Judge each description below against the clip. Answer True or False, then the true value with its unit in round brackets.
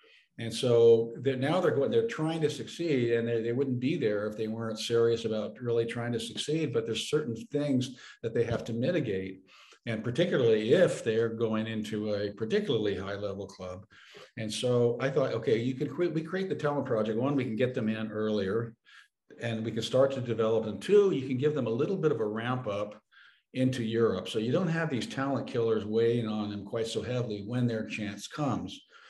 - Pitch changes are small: False (3.6 semitones)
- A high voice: False (115 Hz)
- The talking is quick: True (210 wpm)